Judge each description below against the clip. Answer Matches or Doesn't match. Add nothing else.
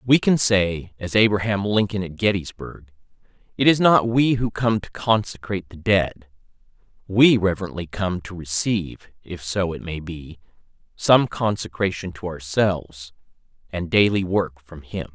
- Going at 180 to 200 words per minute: Doesn't match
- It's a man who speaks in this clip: Matches